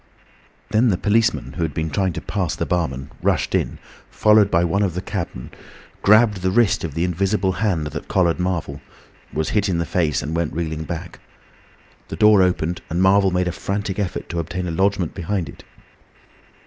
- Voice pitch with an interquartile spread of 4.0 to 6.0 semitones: No, average, 3.3 semitones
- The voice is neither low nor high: No, very low, 90 Hz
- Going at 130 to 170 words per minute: No, average, 190 wpm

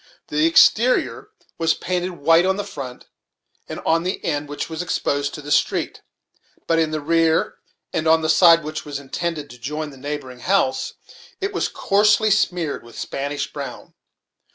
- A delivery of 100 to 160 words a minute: No, average, 170 wpm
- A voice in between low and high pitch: Yes, medium, 160 Hz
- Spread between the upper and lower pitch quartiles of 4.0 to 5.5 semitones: No, average, 3.4 semitones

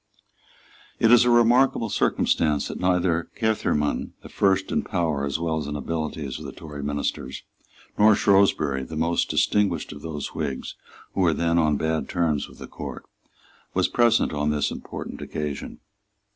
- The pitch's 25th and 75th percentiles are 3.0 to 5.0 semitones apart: Yes, average, 4.7 semitones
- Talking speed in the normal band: Yes, average, 160 wpm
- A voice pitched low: Yes, very low, 80 Hz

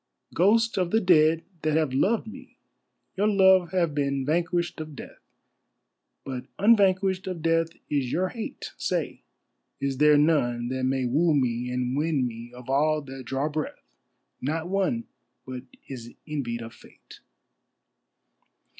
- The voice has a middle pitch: Yes, medium, 155 Hz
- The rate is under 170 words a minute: Yes, average, 145 wpm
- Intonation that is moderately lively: No, wide, 5.7 semitones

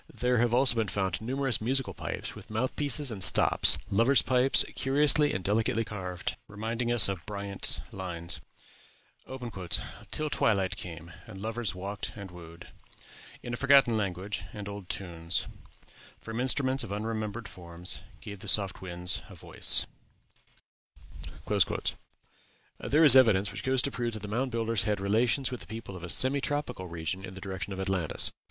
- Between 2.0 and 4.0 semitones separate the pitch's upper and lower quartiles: No, average, 4.6 semitones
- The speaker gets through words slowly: No, average, 160 wpm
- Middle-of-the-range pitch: No, low, 105 Hz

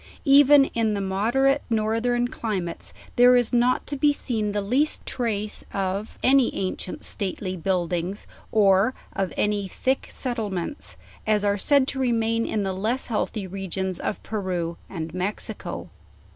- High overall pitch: Yes, high, 215 Hz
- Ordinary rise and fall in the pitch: Yes, average, 4.3 semitones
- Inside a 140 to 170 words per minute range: Yes, average, 145 wpm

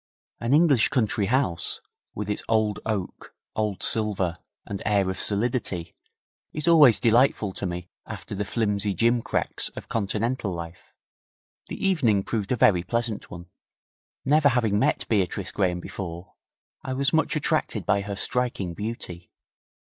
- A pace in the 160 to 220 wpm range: No, average, 140 wpm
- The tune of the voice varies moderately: Yes, average, 4.1 semitones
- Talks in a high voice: No, low, 105 Hz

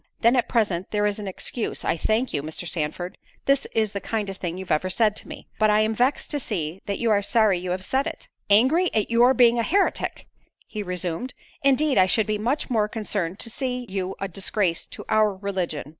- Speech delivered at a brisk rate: Yes, fast, 210 wpm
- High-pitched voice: Yes, high, 210 Hz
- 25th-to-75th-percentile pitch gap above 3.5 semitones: Yes, average, 4.1 semitones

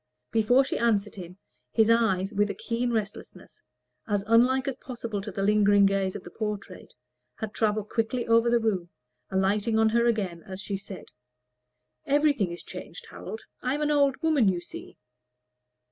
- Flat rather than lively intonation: No, average, 3.2 semitones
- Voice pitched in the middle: No, high, 220 Hz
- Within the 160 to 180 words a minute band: Yes, average, 165 wpm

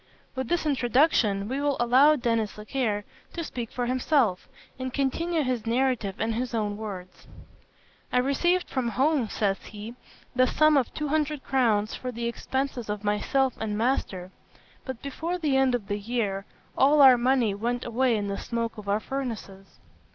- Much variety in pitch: No, average, 4.1 semitones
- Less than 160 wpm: No, average, 170 wpm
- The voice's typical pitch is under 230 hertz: No, high, 245 Hz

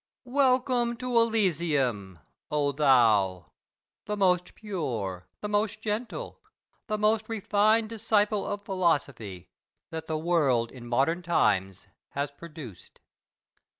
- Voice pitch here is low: No, medium, 170 Hz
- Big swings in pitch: Yes, wide, 8.7 semitones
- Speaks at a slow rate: Yes, slow, 110 wpm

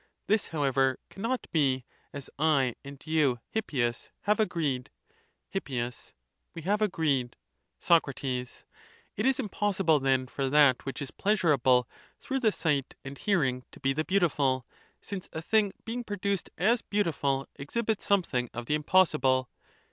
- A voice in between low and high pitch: Yes, medium, 150 Hz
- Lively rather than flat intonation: Yes, wide, 7.1 semitones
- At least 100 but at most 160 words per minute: Yes, average, 140 wpm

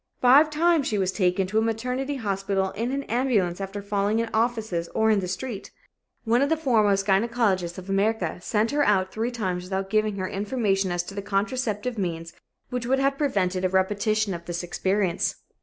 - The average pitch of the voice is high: Yes, high, 205 Hz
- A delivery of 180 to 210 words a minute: Yes, average, 190 wpm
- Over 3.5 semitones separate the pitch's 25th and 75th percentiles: Yes, average, 3.9 semitones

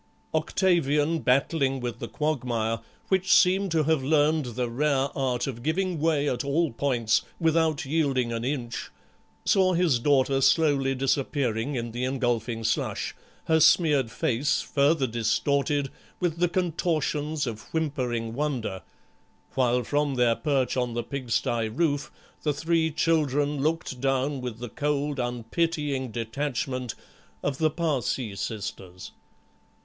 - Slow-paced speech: Yes, slow, 130 wpm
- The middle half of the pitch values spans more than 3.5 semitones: Yes, average, 4.2 semitones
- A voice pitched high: No, medium, 140 Hz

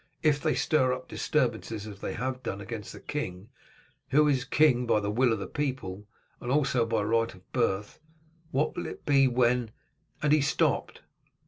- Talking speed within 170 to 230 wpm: Yes, average, 190 wpm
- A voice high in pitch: No, low, 125 Hz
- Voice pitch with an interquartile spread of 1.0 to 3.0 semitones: No, average, 4.3 semitones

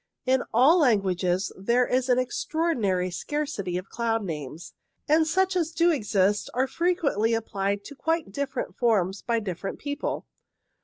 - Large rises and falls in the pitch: Yes, wide, 7.2 semitones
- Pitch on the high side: Yes, high, 235 Hz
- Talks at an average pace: Yes, average, 145 wpm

